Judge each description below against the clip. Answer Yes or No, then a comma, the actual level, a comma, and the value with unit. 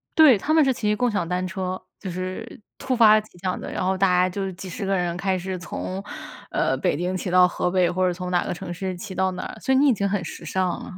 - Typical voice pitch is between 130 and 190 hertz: Yes, medium, 185 Hz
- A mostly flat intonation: Yes, narrow, 2.3 semitones